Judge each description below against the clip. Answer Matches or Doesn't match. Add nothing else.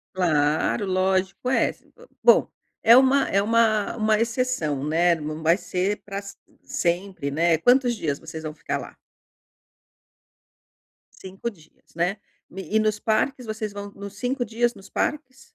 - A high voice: Matches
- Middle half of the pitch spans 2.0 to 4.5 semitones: Doesn't match